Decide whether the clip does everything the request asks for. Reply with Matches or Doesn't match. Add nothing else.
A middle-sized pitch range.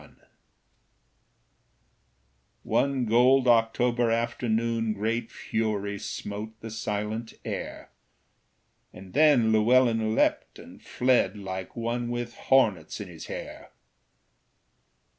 Doesn't match